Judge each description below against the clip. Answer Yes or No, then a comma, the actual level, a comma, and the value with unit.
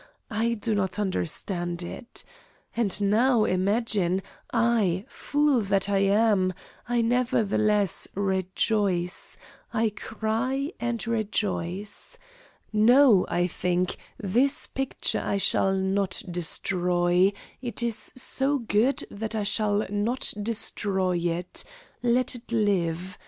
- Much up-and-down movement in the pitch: No, average, 3.7 semitones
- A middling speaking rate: No, slow, 110 wpm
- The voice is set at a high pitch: Yes, high, 205 Hz